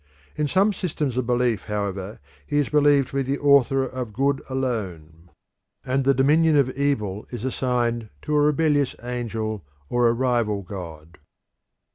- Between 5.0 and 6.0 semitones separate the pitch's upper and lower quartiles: No, average, 4.6 semitones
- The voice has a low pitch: Yes, low, 125 Hz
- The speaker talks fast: No, average, 155 wpm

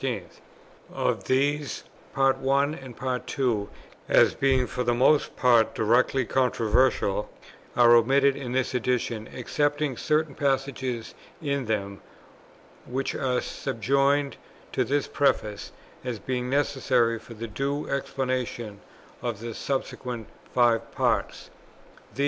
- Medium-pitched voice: No, low, 130 Hz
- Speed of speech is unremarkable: No, slow, 115 wpm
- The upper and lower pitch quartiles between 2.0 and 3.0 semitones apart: Yes, average, 2.7 semitones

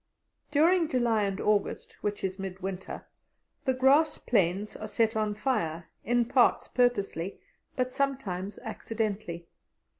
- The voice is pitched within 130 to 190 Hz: No, high, 215 Hz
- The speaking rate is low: Yes, slow, 125 wpm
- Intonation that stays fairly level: No, average, 4.6 semitones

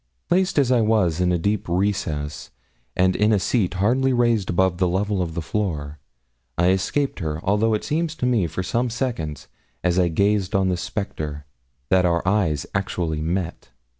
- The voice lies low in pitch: Yes, very low, 95 Hz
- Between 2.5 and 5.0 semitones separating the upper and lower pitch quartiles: Yes, average, 4.1 semitones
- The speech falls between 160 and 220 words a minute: Yes, average, 180 wpm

